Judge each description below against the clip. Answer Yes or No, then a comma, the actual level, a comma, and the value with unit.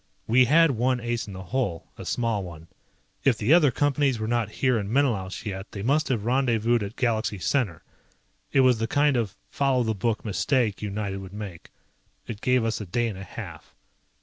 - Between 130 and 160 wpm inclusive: No, average, 200 wpm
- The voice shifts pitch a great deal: No, average, 4.0 semitones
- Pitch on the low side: Yes, low, 115 Hz